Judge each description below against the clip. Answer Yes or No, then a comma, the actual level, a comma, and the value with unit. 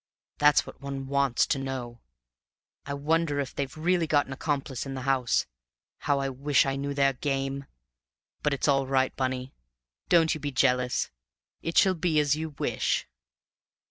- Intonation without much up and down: Yes, narrow, 1.8 semitones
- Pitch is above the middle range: No, medium, 140 Hz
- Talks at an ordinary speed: Yes, average, 170 wpm